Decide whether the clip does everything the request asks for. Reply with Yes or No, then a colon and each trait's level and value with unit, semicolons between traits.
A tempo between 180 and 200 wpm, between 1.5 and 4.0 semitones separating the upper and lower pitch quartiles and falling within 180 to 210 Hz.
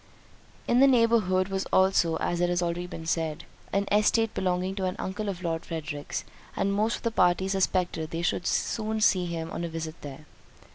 Yes: average, 195 wpm; average, 3.1 semitones; medium, 185 Hz